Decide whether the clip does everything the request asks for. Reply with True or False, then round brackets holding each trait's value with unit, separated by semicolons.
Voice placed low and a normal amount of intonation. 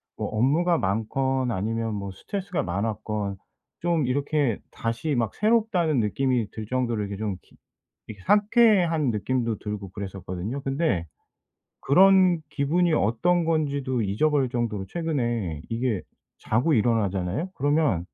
False (125 Hz; 7.0 semitones)